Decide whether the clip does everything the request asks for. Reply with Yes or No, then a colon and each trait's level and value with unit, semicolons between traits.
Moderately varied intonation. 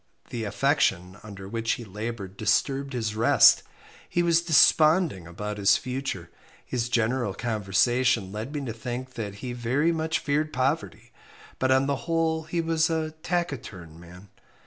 No: wide, 6.4 semitones